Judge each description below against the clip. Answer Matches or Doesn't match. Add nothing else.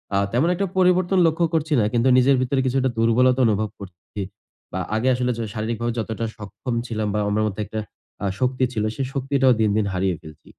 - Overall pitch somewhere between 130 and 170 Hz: Doesn't match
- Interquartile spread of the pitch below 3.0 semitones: Doesn't match